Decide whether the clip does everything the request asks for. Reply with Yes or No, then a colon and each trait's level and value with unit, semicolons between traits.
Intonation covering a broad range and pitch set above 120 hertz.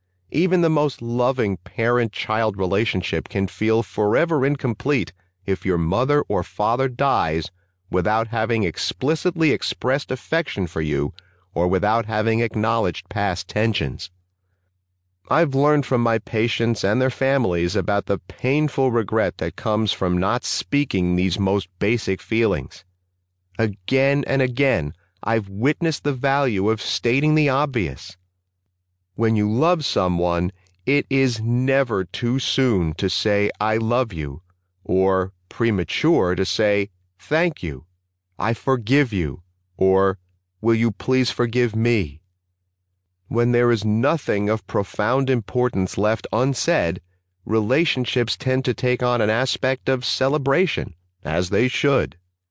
No: wide, 5.7 semitones; low, 110 Hz